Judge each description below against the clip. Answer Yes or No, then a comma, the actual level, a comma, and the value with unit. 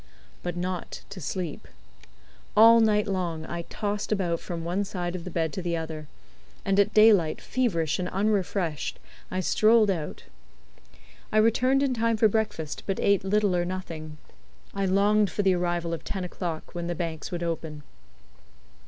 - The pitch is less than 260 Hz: Yes, medium, 185 Hz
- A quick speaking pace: No, average, 165 wpm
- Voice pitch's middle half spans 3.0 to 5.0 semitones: Yes, average, 3.7 semitones